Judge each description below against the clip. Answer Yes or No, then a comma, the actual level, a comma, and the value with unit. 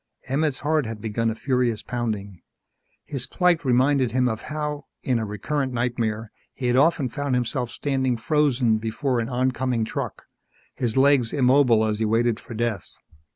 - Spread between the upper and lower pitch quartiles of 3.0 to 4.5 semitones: Yes, average, 3.3 semitones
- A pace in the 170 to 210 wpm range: No, average, 160 wpm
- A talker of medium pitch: No, low, 125 Hz